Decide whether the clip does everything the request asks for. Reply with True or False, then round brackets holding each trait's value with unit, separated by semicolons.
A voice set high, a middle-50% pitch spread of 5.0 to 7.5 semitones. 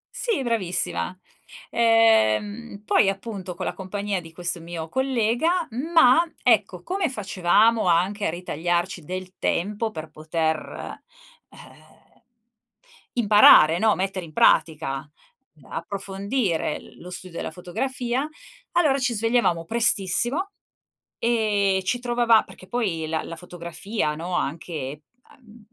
True (195 Hz; 5.3 semitones)